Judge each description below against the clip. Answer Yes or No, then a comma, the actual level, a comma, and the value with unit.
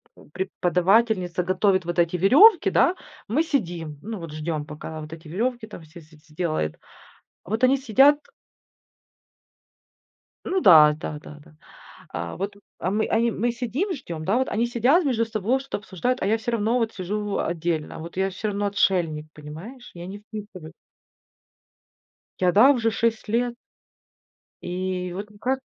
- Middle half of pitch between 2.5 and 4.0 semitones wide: No, wide, 5.6 semitones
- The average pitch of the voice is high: Yes, high, 195 Hz